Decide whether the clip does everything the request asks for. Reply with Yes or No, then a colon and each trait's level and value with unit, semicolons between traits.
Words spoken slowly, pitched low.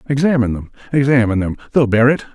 Yes: slow, 130 wpm; low, 125 Hz